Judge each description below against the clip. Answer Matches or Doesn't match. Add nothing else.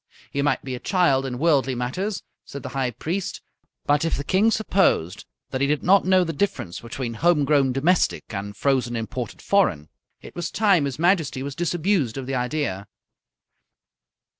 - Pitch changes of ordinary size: Doesn't match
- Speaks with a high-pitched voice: Doesn't match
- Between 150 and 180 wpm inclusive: Matches